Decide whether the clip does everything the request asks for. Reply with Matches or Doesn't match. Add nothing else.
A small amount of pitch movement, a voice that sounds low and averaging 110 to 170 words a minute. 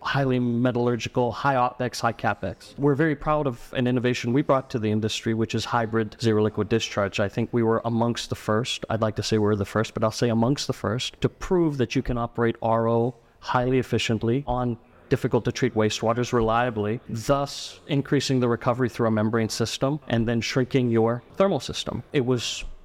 Doesn't match